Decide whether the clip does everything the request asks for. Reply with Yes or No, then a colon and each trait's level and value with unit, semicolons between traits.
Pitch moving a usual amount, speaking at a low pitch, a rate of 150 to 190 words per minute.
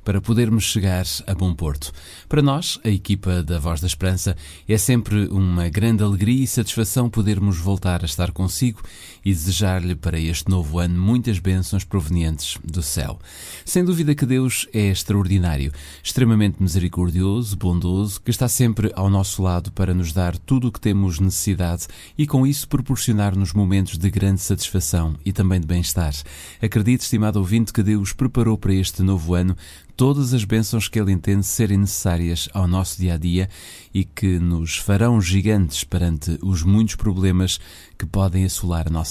Yes: average, 3.5 semitones; very low, 95 Hz; average, 165 wpm